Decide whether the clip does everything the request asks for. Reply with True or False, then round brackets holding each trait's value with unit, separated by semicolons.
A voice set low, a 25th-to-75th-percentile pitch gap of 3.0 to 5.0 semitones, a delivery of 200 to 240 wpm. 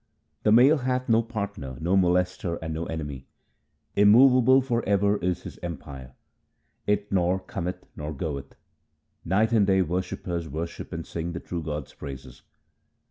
False (90 Hz; 4.5 semitones; 145 wpm)